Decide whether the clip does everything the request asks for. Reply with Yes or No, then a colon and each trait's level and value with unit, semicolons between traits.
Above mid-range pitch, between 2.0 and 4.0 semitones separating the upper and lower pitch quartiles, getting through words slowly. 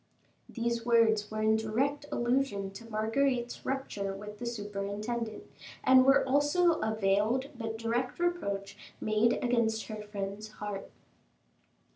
Yes: high, 225 Hz; average, 3.2 semitones; slow, 125 wpm